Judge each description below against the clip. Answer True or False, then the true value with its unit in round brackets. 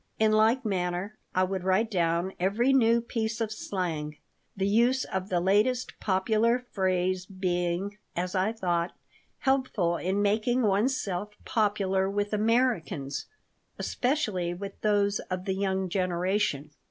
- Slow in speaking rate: True (130 wpm)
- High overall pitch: True (195 Hz)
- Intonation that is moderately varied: True (3.2 semitones)